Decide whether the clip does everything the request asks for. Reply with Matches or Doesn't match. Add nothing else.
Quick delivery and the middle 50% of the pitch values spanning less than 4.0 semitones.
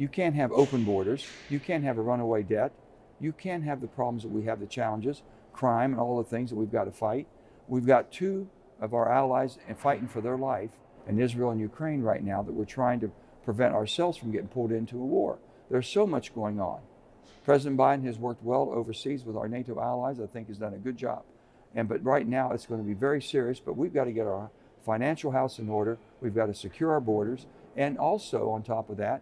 Matches